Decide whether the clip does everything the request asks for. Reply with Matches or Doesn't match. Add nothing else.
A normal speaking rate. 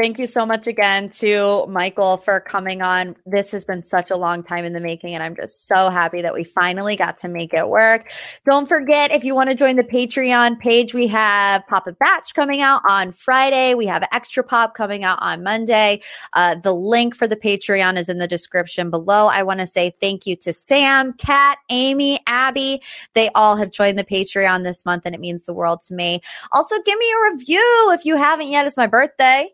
Doesn't match